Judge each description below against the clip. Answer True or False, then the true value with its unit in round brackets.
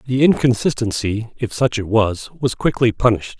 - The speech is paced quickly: False (160 wpm)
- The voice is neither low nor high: False (115 Hz)